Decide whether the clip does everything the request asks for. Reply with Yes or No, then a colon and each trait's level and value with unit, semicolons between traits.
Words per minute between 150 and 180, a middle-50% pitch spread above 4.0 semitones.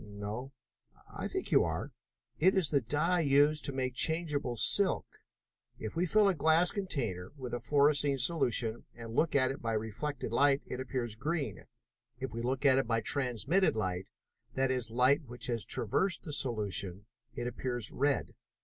Yes: average, 170 wpm; average, 4.4 semitones